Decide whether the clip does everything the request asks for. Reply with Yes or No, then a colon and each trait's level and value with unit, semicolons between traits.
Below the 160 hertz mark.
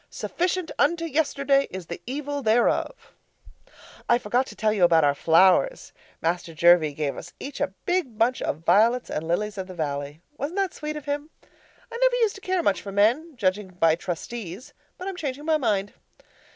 No: high, 230 Hz